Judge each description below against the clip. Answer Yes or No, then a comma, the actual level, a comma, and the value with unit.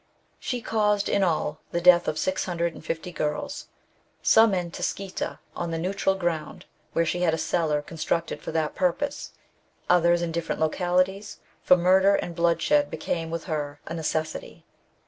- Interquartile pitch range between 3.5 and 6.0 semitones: No, average, 2.7 semitones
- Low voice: No, medium, 175 Hz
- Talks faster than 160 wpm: No, average, 155 wpm